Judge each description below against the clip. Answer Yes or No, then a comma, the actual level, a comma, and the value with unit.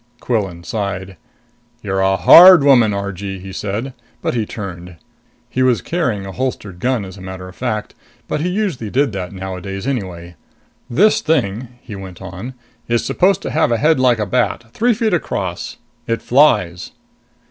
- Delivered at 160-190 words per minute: Yes, average, 170 wpm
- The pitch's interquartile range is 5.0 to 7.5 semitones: Yes, average, 5.3 semitones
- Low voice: Yes, low, 105 Hz